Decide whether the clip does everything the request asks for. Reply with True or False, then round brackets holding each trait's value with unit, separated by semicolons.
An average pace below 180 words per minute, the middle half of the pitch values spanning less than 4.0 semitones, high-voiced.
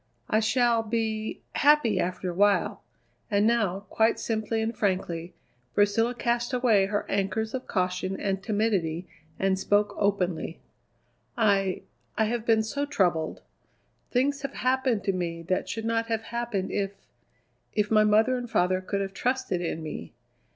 True (150 wpm; 3.3 semitones; 210 Hz)